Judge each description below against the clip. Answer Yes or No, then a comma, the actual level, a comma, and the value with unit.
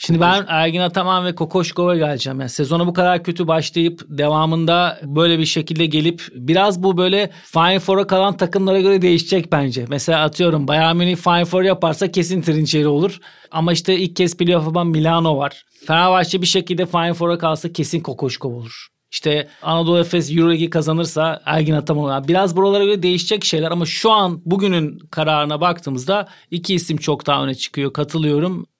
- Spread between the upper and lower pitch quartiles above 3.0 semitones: No, average, 2.7 semitones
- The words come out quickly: Yes, fast, 165 wpm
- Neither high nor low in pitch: Yes, medium, 170 Hz